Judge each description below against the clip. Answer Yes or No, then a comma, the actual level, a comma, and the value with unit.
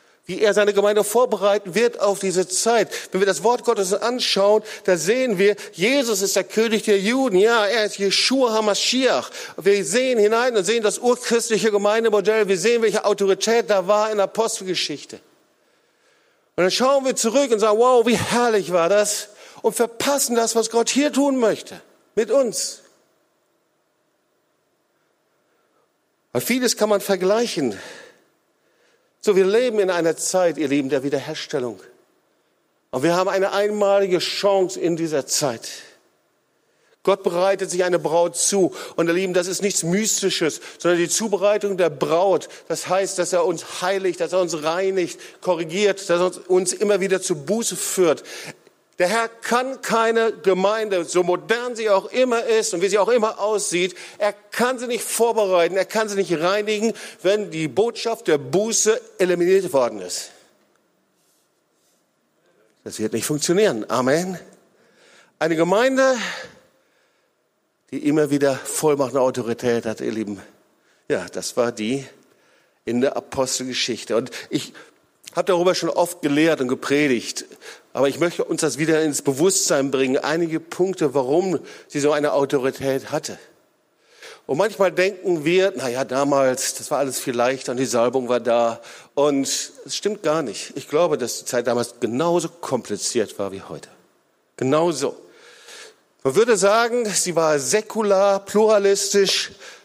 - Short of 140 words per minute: No, average, 155 wpm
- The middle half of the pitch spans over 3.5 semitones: Yes, average, 4.9 semitones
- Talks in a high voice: Yes, high, 195 Hz